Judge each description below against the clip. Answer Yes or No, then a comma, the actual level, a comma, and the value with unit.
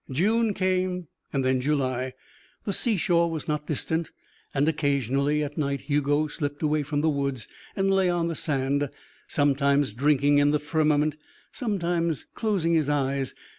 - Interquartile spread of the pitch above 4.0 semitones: No, average, 3.2 semitones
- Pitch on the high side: No, medium, 150 Hz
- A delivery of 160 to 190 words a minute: No, average, 150 wpm